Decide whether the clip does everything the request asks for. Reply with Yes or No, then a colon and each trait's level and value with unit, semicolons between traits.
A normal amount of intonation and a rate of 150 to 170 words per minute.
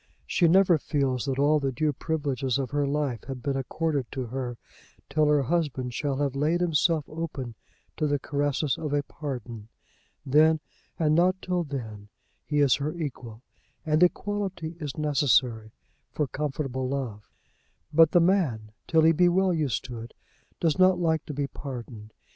Yes: average, 3.6 semitones; average, 165 wpm